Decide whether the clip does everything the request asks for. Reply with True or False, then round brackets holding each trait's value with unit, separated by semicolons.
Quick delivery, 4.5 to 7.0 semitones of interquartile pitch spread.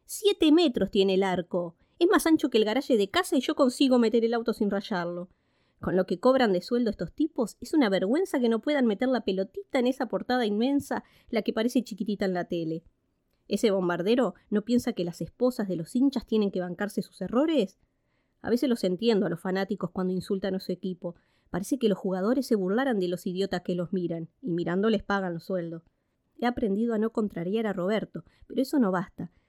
True (210 wpm; 5.0 semitones)